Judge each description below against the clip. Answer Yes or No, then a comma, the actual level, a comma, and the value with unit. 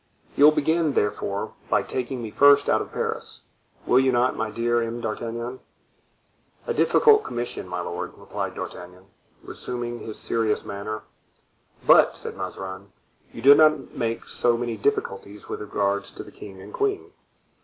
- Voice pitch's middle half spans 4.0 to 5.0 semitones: Yes, average, 4.6 semitones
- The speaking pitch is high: No, low, 115 Hz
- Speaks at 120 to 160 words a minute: Yes, average, 155 wpm